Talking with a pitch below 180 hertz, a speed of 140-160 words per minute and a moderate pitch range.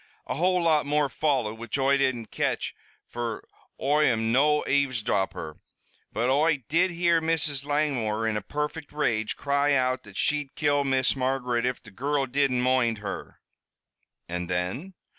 Yes: low, 135 Hz; average, 155 wpm; average, 4.2 semitones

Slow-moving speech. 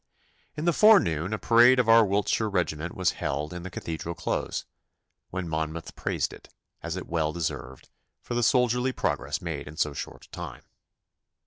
No: average, 175 wpm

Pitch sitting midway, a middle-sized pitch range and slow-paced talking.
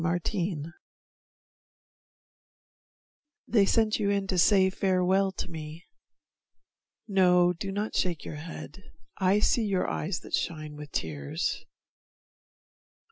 Yes: medium, 180 Hz; average, 3.3 semitones; slow, 110 wpm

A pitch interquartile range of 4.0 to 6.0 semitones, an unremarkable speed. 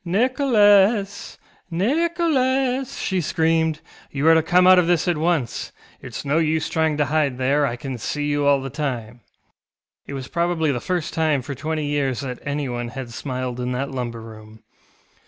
Yes: average, 5.2 semitones; average, 175 wpm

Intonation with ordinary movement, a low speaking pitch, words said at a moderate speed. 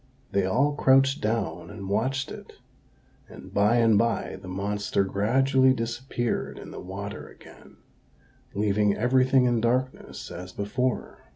No: average, 4.3 semitones; low, 115 Hz; slow, 130 wpm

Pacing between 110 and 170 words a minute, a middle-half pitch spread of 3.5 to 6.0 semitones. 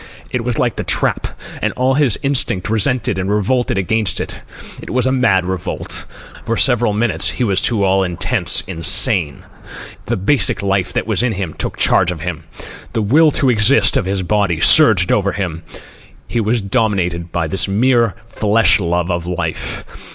No: average, 180 wpm; average, 4.6 semitones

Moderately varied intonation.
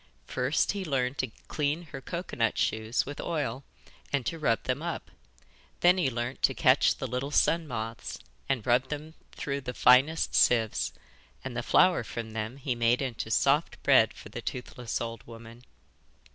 Yes: average, 3.8 semitones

